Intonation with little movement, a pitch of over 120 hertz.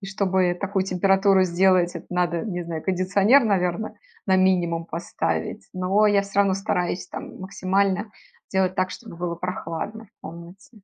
Yes: narrow, 1.9 semitones; medium, 185 Hz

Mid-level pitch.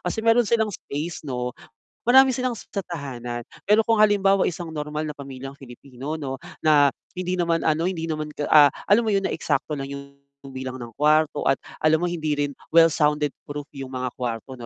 Yes: medium, 150 Hz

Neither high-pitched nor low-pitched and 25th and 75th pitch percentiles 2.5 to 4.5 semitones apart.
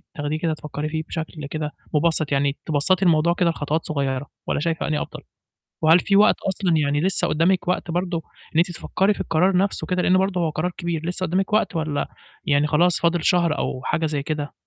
Yes: medium, 165 Hz; average, 2.9 semitones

